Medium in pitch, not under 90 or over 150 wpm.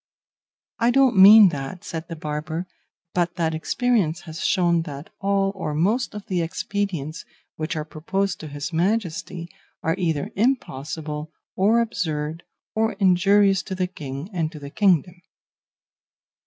Yes: medium, 175 Hz; average, 140 wpm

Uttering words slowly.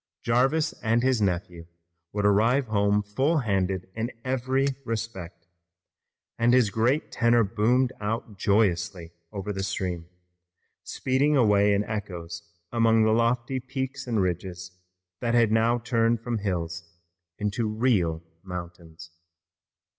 Yes: slow, 125 wpm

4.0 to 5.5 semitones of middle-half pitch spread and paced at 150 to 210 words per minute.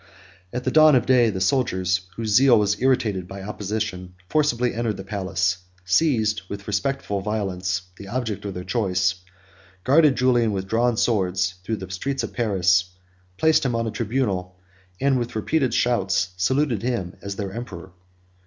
Yes: average, 4.6 semitones; average, 160 wpm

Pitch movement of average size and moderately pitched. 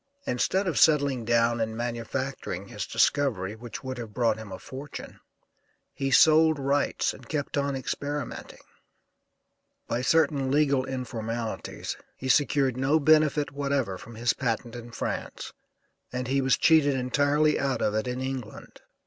No: average, 3.3 semitones; low, 130 Hz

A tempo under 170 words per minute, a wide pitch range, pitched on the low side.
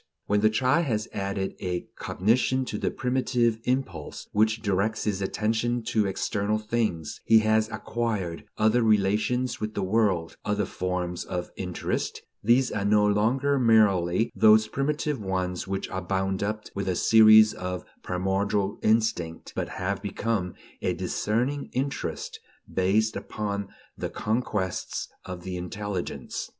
No: average, 140 wpm; average, 2.9 semitones; low, 105 Hz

